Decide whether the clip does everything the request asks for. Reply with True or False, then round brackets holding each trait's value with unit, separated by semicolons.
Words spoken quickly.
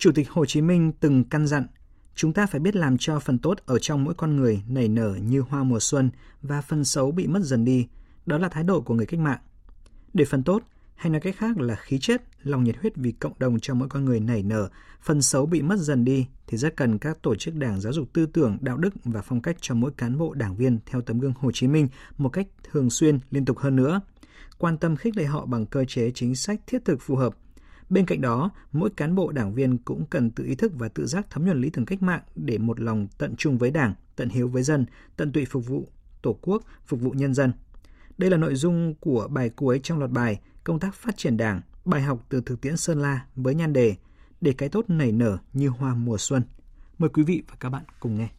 True (255 wpm)